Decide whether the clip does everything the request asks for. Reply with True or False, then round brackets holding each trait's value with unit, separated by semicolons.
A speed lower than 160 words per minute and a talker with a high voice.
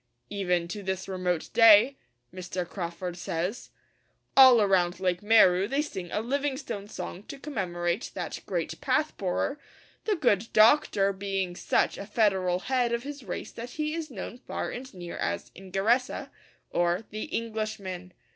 True (150 wpm; 200 Hz)